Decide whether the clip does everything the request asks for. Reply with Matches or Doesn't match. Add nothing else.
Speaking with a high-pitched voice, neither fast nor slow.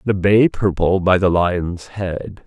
Doesn't match